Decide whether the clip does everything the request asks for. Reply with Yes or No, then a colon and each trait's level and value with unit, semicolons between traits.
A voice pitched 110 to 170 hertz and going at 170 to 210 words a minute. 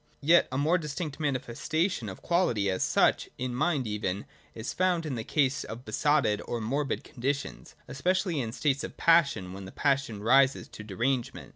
Yes: low, 135 Hz; average, 180 wpm